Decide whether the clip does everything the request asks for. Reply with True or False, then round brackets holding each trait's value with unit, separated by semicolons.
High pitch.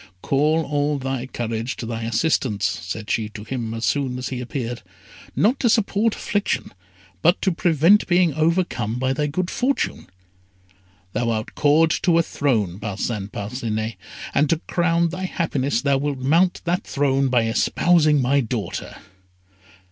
False (135 Hz)